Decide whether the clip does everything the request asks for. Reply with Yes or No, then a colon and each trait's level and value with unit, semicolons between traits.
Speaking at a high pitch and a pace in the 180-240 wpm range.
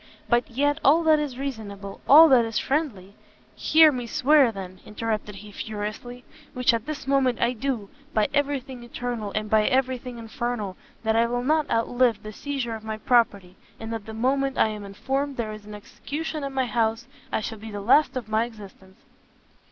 Yes: high, 235 Hz; average, 195 wpm